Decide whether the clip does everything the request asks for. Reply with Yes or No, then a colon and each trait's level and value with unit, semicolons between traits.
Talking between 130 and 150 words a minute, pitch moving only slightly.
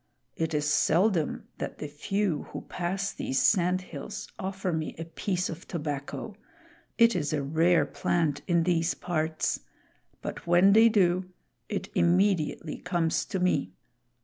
No: average, 145 wpm; average, 3.2 semitones